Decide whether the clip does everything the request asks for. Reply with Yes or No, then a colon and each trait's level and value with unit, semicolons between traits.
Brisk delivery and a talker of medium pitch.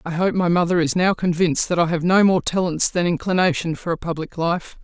Yes: fast, 235 wpm; medium, 175 Hz